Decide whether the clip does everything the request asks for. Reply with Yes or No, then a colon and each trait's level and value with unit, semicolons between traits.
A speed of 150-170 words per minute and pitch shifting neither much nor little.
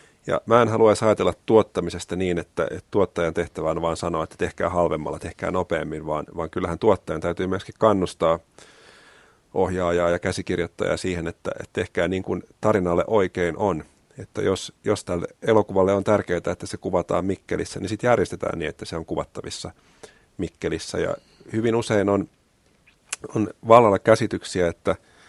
Yes: fast, 155 wpm; average, 3.3 semitones